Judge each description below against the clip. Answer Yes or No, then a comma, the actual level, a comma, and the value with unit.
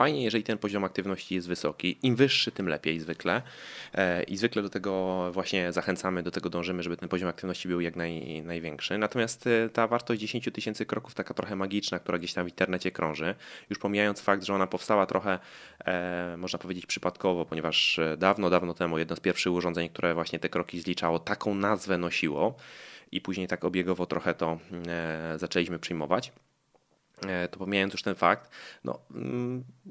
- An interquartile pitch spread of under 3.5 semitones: Yes, average, 2.7 semitones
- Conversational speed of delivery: No, fast, 170 wpm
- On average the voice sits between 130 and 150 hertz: No, very low, 90 Hz